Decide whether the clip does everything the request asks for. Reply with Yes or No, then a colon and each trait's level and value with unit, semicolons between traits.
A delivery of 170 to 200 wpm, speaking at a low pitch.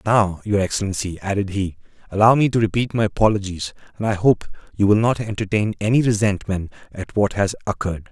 Yes: average, 185 wpm; low, 100 Hz